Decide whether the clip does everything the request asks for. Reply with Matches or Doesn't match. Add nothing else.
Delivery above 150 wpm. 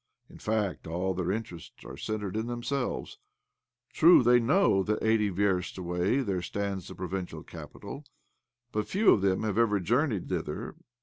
Matches